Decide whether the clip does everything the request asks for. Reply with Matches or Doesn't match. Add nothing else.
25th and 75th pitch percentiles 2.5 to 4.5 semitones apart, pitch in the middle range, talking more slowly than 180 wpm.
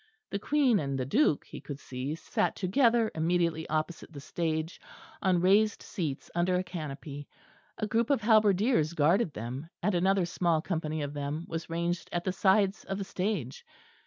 Matches